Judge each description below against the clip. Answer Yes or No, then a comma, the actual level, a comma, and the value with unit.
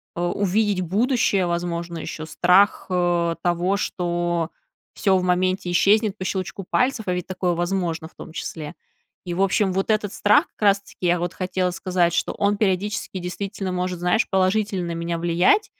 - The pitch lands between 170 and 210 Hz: Yes, medium, 185 Hz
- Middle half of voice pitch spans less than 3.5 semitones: Yes, narrow, 2.4 semitones